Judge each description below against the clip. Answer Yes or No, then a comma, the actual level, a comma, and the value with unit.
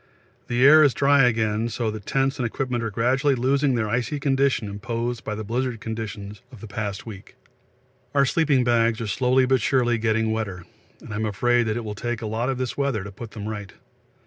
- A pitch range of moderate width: Yes, average, 3.1 semitones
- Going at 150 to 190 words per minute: No, fast, 205 wpm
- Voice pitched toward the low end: Yes, low, 115 Hz